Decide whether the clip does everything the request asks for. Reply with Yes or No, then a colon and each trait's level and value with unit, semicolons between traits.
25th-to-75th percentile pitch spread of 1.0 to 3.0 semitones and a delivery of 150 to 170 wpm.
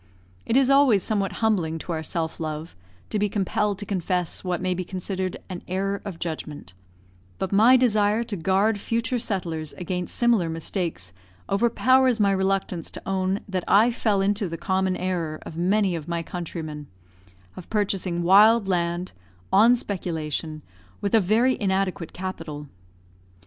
No: average, 3.5 semitones; average, 155 wpm